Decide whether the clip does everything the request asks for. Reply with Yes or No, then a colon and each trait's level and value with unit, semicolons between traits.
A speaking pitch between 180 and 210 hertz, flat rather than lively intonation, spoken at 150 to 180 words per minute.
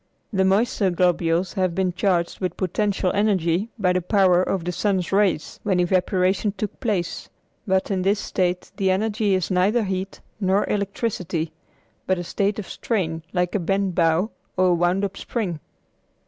Yes: high, 190 Hz; narrow, 2.1 semitones; average, 165 wpm